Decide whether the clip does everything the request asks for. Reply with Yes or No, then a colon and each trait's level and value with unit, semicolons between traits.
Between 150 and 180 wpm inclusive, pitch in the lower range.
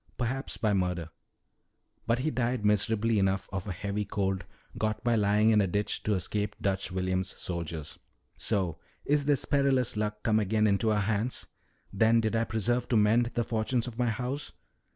Yes: average, 175 wpm; low, 110 Hz